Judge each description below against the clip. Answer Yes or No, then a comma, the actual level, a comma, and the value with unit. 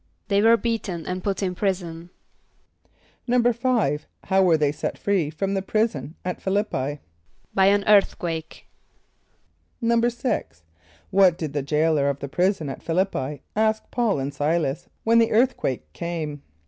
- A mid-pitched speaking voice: Yes, medium, 180 Hz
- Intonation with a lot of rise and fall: Yes, wide, 6.1 semitones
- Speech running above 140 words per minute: Yes, average, 150 wpm